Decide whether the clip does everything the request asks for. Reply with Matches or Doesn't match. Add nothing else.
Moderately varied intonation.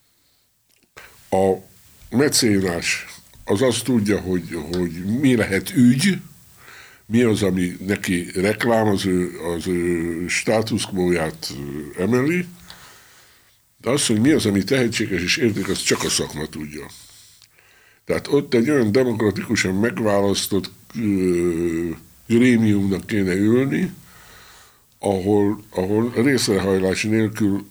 Matches